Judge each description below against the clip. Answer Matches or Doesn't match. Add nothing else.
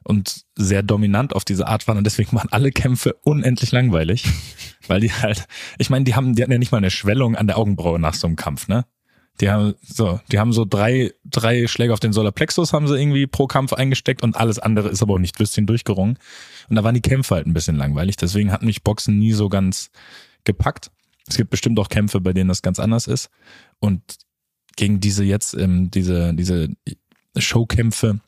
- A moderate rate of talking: Doesn't match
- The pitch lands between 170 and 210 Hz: Doesn't match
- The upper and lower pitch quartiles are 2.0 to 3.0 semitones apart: Doesn't match